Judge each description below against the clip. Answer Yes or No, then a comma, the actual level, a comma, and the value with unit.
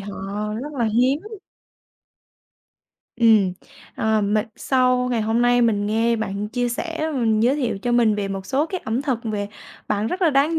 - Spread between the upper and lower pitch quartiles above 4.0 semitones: No, average, 3.5 semitones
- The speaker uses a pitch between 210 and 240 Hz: Yes, high, 235 Hz